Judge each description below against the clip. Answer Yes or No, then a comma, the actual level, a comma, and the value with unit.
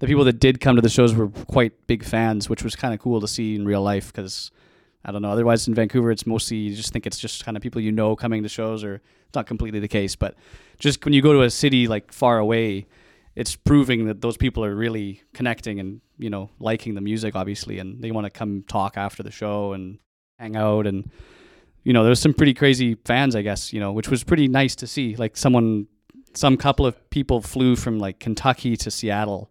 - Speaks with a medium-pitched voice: No, low, 110 Hz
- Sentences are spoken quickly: Yes, fast, 240 wpm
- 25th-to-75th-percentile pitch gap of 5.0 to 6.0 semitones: No, average, 3.0 semitones